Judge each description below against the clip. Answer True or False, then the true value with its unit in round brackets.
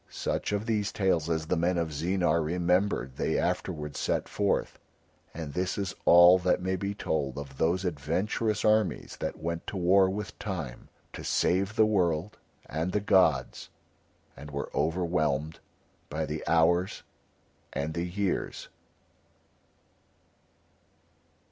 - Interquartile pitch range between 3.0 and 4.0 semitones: True (3.6 semitones)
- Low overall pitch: True (85 Hz)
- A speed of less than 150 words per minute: True (135 wpm)